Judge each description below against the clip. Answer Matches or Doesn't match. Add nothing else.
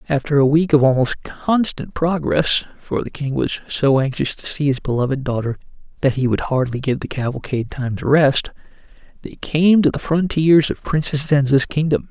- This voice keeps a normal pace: Matches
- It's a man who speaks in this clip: Matches